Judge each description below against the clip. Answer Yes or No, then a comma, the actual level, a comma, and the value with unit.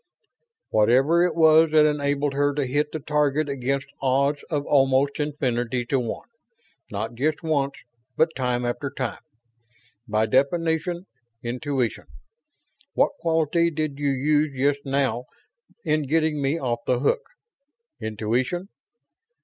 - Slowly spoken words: Yes, slow, 125 wpm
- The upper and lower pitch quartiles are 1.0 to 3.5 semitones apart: Yes, average, 3.2 semitones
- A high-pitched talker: No, medium, 140 Hz